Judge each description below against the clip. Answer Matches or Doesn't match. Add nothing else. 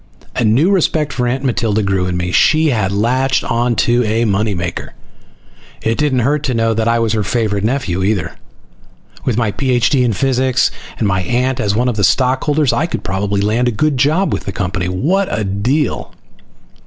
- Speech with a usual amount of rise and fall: Matches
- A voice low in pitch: Matches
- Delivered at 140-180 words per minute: Doesn't match